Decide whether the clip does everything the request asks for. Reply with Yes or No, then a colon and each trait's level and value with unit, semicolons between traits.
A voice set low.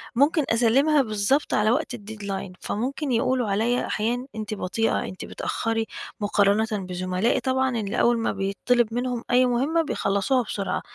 No: high, 225 Hz